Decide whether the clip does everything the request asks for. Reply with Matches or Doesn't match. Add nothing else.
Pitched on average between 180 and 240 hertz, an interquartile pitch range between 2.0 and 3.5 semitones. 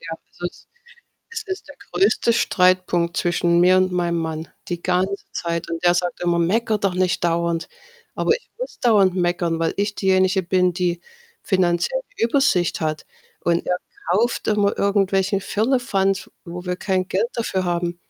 Matches